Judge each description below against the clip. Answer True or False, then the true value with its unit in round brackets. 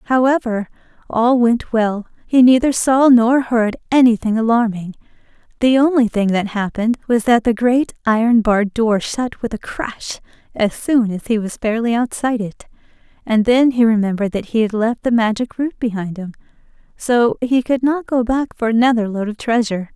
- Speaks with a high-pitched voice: True (230 Hz)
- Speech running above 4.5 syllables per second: True (5.0 syllables/s)